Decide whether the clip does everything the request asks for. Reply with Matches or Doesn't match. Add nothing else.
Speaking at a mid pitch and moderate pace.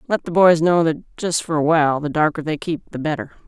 Doesn't match